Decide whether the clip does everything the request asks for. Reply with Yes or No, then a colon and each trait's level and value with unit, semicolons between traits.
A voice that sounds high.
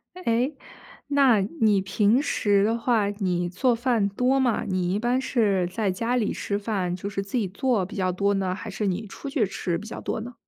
Yes: high, 210 Hz